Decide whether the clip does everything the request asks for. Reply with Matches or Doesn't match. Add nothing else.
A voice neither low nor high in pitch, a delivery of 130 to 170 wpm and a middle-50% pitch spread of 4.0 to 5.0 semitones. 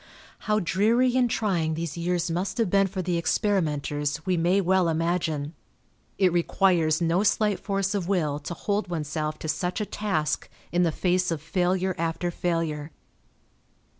Doesn't match